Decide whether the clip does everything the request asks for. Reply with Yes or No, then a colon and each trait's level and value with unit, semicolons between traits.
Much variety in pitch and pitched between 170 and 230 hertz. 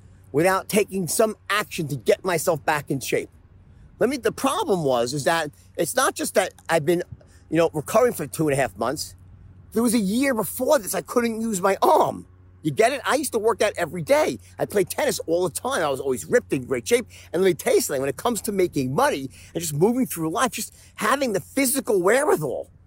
Yes: wide, 7.2 semitones; medium, 185 Hz